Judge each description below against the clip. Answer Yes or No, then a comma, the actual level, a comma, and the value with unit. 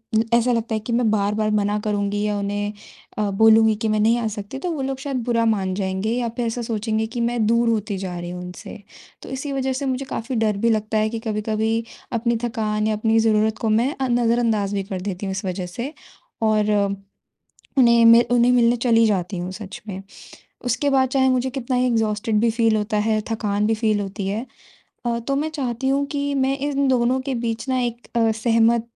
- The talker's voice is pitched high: Yes, high, 225 Hz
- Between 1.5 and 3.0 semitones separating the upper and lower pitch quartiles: Yes, narrow, 2.4 semitones